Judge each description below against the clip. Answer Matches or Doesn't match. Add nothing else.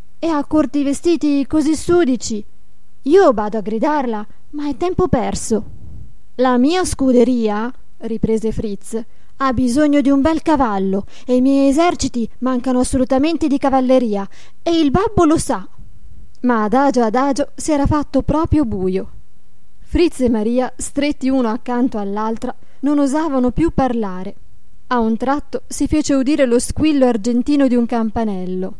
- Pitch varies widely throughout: Doesn't match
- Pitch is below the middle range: Doesn't match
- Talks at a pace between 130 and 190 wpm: Matches